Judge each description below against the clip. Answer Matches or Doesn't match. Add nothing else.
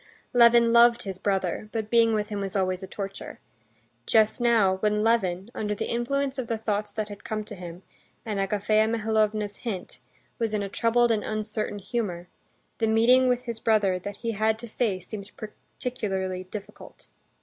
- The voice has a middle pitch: Doesn't match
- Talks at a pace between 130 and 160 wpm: Doesn't match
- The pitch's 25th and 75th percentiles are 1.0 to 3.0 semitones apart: Matches